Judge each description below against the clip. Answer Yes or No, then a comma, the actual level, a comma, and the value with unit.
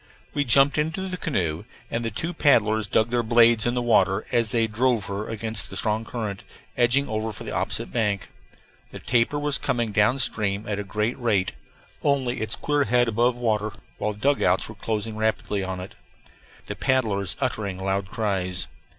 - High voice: No, low, 110 Hz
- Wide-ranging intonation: No, average, 3.0 semitones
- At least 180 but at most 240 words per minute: Yes, average, 185 wpm